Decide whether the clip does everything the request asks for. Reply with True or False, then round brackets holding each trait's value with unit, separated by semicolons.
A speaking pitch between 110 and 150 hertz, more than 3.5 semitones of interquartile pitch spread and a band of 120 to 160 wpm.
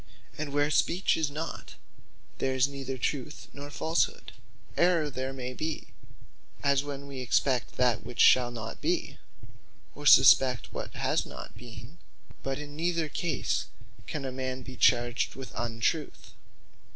False (135 Hz; 2.7 semitones; 145 wpm)